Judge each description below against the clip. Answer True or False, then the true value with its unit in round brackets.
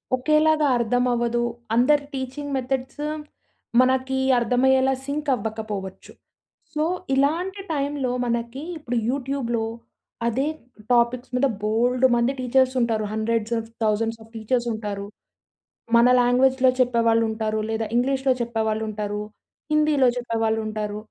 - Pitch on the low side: False (245 Hz)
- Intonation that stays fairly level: False (3.0 semitones)